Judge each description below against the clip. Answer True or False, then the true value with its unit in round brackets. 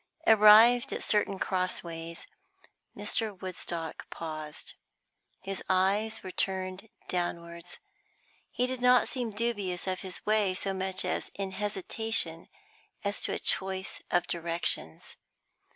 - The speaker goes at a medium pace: False (120 wpm)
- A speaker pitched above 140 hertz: True (190 Hz)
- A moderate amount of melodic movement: True (3.2 semitones)